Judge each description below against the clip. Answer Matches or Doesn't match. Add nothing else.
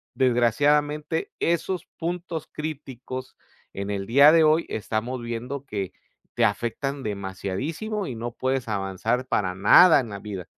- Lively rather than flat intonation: Matches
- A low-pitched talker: Matches